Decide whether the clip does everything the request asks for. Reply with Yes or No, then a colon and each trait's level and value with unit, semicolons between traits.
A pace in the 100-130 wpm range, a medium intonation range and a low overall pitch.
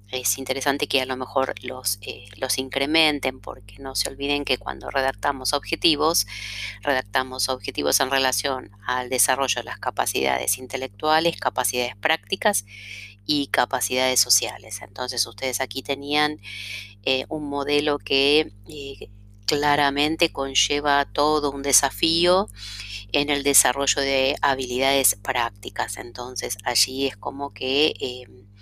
Yes: slow, 125 wpm; average, 3.3 semitones; low, 130 Hz